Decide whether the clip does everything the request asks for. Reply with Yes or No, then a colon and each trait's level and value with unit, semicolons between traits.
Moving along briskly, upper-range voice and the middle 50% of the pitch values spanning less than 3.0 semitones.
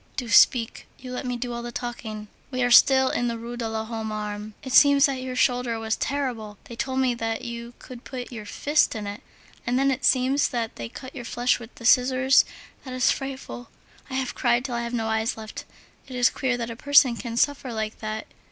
Yes: fast, 225 wpm; high, 245 Hz; narrow, 2.5 semitones